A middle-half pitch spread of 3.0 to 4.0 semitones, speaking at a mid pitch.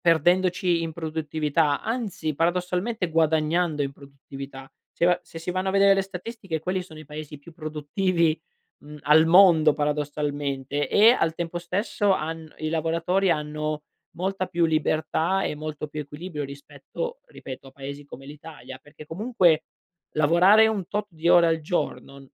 Yes: average, 3.3 semitones; medium, 160 Hz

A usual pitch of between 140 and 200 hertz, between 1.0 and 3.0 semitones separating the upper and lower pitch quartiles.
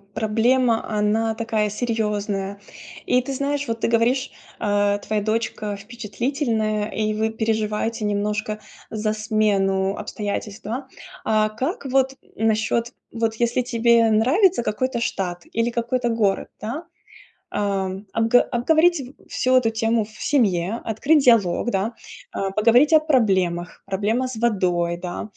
No: high, 220 Hz; narrow, 2.5 semitones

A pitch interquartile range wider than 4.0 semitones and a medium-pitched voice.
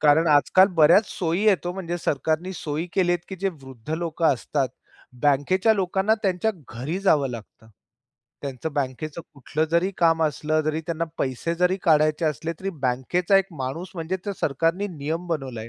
No: average, 3.7 semitones; medium, 160 Hz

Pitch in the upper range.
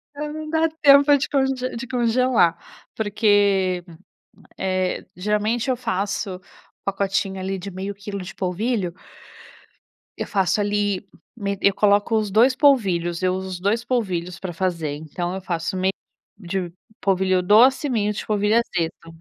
Yes: high, 200 Hz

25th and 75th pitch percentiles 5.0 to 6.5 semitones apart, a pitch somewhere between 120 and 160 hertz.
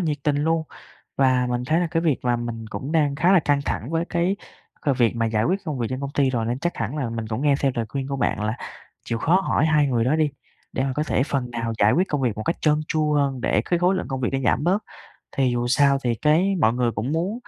No: average, 4.6 semitones; medium, 140 Hz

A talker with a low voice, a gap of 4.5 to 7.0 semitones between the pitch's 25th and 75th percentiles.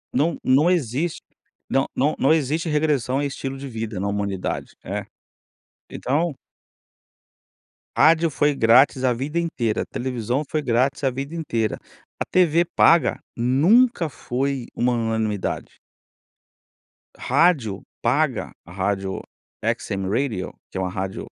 Yes: low, 130 Hz; average, 5.2 semitones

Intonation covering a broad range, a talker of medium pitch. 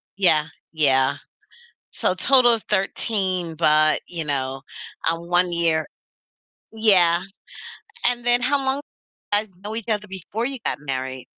Yes: wide, 6.3 semitones; medium, 180 Hz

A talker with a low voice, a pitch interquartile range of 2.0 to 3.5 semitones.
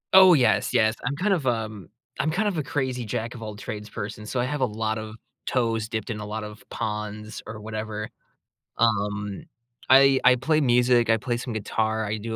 Yes: low, 110 Hz; average, 2.9 semitones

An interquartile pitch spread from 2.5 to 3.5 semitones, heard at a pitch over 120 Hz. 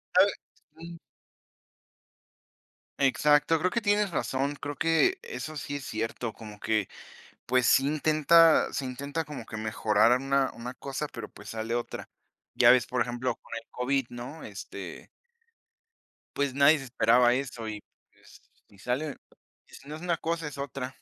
No: average, 4.0 semitones; low, 135 Hz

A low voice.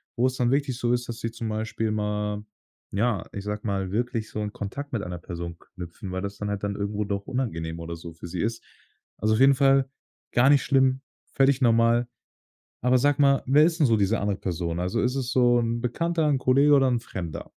Yes: low, 115 Hz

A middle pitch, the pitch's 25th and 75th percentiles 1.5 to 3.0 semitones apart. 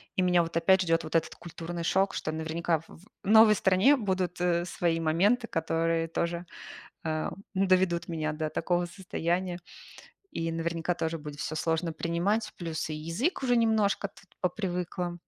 Yes: medium, 170 Hz; narrow, 2.4 semitones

